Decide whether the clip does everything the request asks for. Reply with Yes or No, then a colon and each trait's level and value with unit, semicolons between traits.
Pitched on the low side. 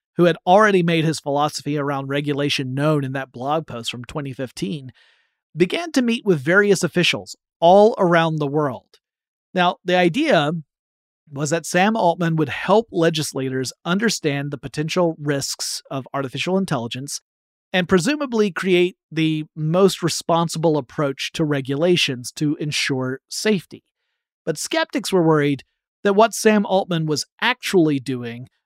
No: medium, 160 Hz